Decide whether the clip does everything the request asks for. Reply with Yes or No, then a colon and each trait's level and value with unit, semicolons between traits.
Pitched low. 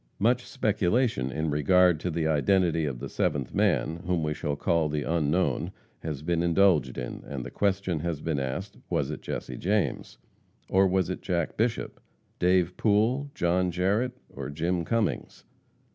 Yes: very low, 85 Hz